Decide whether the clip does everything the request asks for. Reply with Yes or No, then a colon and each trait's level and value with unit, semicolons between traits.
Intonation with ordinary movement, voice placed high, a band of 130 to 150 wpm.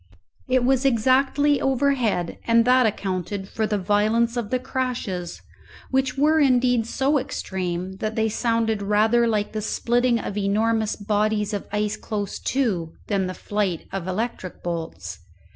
Yes: average, 3.8 semitones; high, 220 Hz; average, 145 wpm